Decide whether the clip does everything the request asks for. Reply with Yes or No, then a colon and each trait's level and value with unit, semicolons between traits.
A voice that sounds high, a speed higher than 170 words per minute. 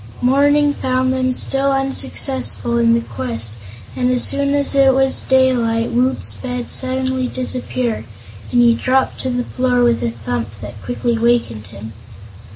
No: very high, 250 Hz; average, 155 wpm